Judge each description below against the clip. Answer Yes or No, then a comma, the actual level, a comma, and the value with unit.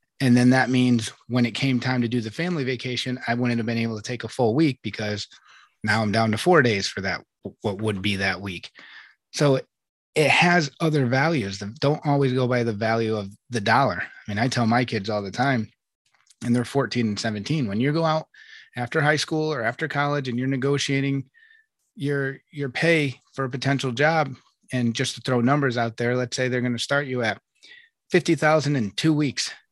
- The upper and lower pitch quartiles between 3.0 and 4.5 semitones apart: Yes, average, 3.7 semitones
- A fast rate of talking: Yes, fast, 215 wpm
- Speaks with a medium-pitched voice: No, low, 125 Hz